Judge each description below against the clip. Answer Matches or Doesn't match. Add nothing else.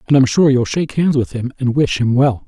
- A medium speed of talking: Doesn't match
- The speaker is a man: Matches